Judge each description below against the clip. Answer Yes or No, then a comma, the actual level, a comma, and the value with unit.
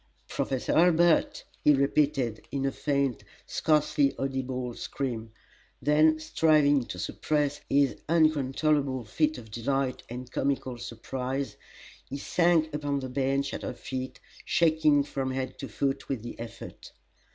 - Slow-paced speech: Yes, slow, 130 wpm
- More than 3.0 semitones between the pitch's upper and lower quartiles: No, narrow, 2.6 semitones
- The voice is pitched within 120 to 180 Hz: Yes, medium, 140 Hz